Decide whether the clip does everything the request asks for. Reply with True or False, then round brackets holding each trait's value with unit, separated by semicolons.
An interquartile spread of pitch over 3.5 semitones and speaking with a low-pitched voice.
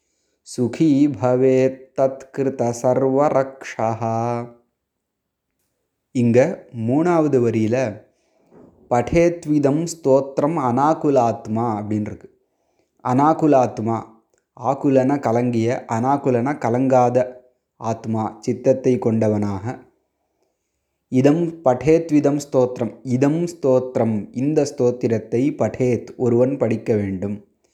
False (2.9 semitones; 125 Hz)